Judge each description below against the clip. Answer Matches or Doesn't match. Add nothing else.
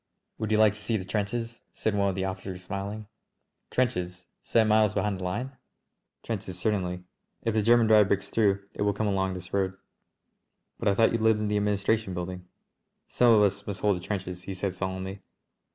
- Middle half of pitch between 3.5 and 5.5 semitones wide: Doesn't match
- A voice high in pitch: Doesn't match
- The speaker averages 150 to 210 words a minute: Matches